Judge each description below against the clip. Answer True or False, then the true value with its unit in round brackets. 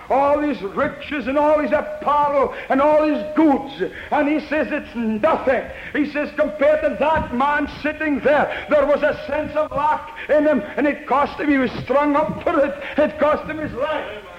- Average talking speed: True (195 wpm)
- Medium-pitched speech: False (295 Hz)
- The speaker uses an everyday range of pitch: False (1.1 semitones)